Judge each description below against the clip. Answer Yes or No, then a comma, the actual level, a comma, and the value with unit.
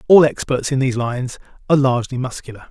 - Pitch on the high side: No, low, 130 Hz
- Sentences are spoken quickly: No, average, 180 wpm